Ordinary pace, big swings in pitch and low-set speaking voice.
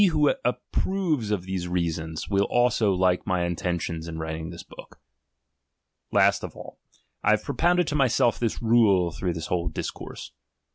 Yes: average, 160 wpm; wide, 6.1 semitones; very low, 95 Hz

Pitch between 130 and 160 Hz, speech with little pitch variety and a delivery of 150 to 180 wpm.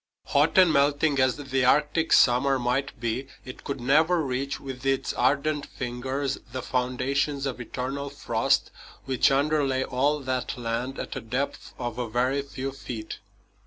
Yes: low, 135 Hz; narrow, 1.9 semitones; average, 155 wpm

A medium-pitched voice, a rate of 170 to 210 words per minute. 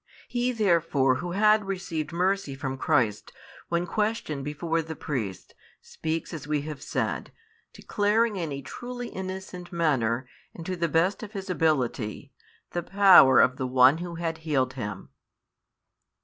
No: medium, 165 Hz; average, 150 wpm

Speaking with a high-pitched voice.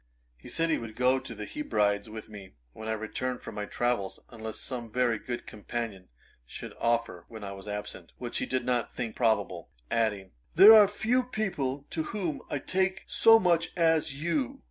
No: low, 125 Hz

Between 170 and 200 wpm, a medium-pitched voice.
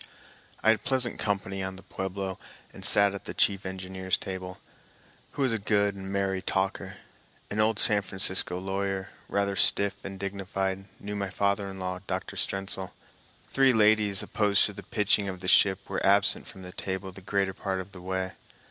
No: average, 180 wpm; very low, 95 Hz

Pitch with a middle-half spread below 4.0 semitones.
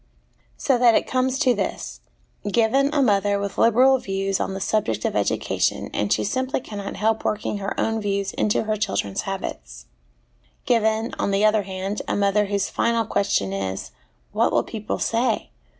Yes: average, 2.9 semitones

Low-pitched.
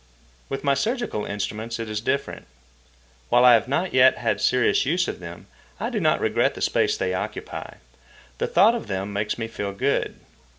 Yes: low, 115 Hz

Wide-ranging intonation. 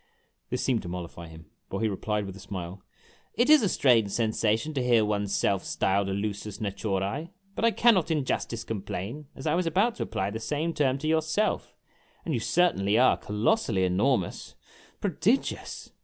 Yes: wide, 7.8 semitones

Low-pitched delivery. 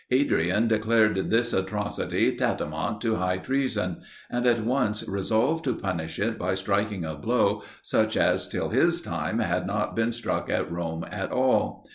Yes: low, 105 Hz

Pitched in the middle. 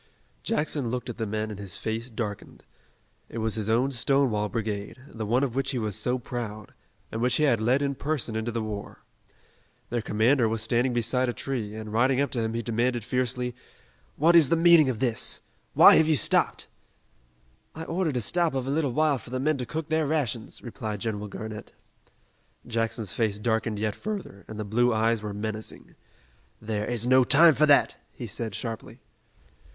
No: low, 120 Hz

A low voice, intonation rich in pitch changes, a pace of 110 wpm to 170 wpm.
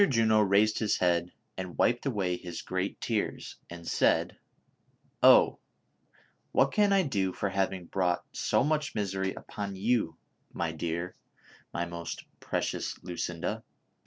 No: very low, 95 Hz; average, 3.8 semitones; average, 140 wpm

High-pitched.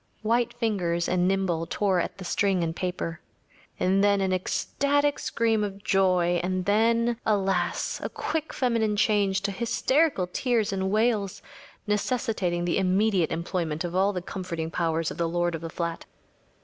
Yes: high, 195 Hz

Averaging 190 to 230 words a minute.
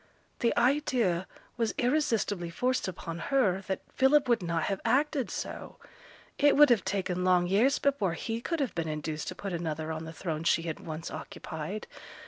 No: average, 175 wpm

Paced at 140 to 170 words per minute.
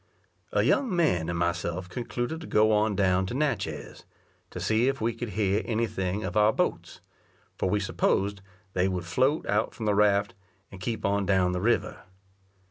No: average, 185 wpm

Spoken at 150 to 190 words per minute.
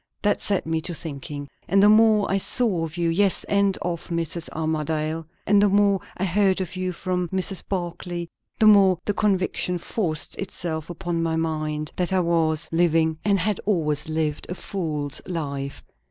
Yes: average, 175 wpm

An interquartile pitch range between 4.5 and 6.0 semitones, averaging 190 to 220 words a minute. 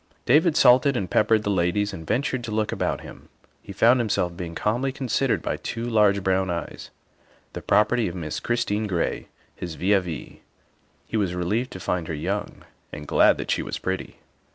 Yes: average, 5.1 semitones; average, 195 wpm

